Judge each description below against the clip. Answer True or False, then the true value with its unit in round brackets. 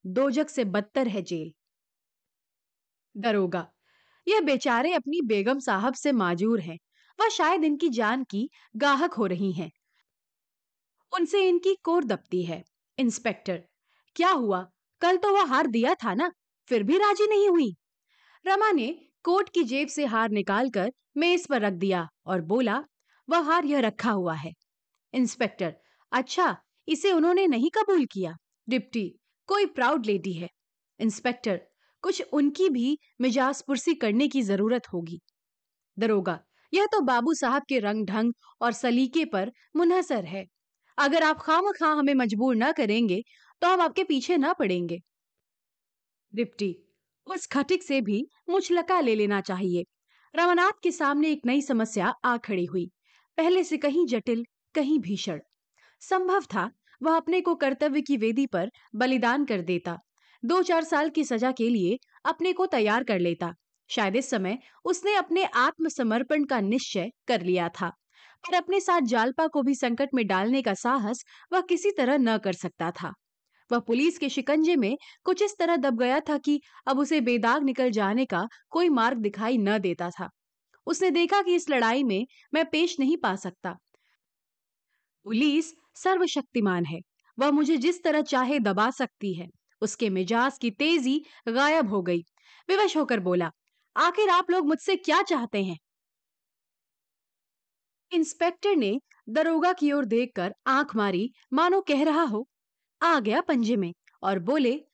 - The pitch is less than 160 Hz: False (255 Hz)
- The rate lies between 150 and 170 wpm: True (155 wpm)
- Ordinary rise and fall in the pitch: False (8.3 semitones)